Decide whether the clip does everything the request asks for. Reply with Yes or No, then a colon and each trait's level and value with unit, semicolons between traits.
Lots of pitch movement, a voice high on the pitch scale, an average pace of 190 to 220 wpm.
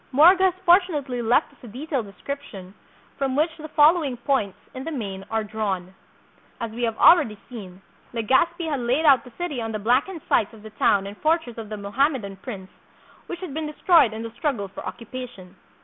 Yes: wide, 6.1 semitones; high, 245 Hz; average, 195 wpm